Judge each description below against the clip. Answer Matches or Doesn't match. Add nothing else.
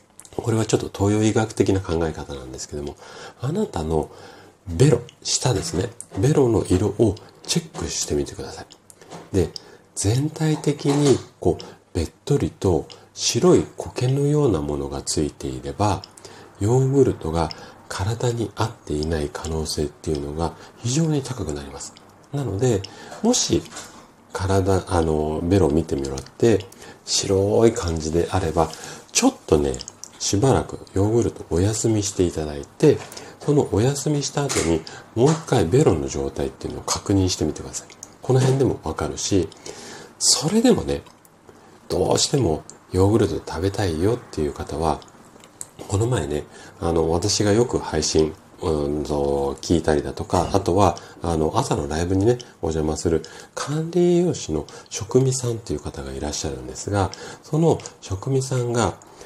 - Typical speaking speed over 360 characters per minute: Doesn't match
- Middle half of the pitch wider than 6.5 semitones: Matches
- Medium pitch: Doesn't match